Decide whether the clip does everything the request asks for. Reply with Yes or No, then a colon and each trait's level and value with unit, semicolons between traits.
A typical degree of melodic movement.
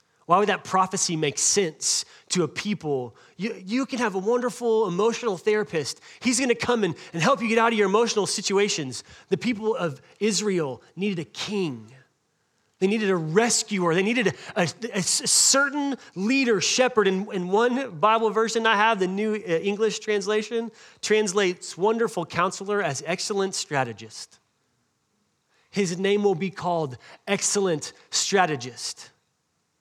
Yes: average, 4.3 semitones